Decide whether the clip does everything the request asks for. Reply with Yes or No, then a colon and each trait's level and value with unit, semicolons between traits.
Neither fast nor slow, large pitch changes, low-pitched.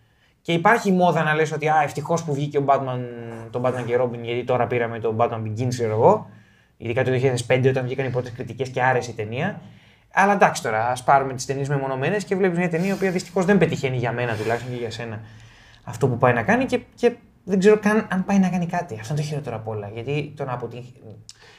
No: fast, 230 wpm; wide, 5.7 semitones; low, 130 Hz